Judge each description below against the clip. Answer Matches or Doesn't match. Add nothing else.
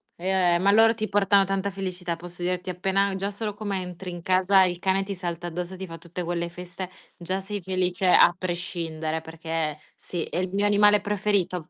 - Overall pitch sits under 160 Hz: Doesn't match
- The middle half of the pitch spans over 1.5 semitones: Matches